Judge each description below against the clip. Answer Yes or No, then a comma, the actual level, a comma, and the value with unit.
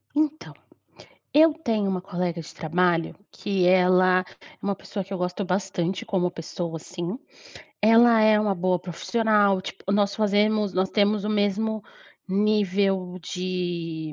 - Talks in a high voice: Yes, high, 195 Hz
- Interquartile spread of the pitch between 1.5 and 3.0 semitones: Yes, average, 2.7 semitones